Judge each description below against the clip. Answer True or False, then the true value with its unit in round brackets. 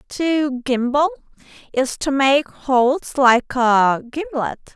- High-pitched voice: True (270 Hz)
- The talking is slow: True (115 wpm)